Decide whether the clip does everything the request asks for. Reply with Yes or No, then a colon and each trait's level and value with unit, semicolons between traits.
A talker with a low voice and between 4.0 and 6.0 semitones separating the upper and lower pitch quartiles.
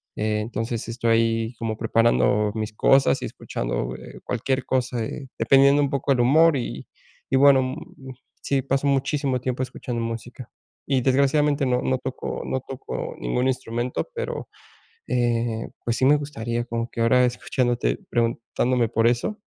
No: low, 125 Hz; average, 2.7 semitones